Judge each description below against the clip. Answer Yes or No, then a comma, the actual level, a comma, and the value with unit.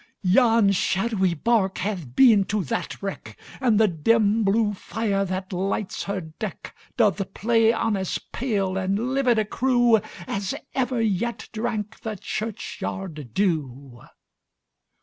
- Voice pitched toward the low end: No, high, 205 Hz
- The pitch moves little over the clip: No, average, 3.2 semitones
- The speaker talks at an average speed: No, slow, 120 wpm